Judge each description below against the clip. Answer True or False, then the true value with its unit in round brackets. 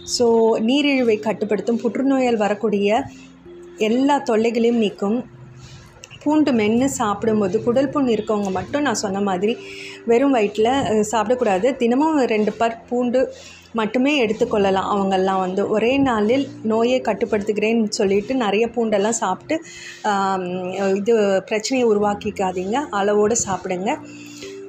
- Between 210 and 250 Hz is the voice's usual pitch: True (220 Hz)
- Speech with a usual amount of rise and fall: True (3.4 semitones)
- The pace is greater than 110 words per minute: False (100 wpm)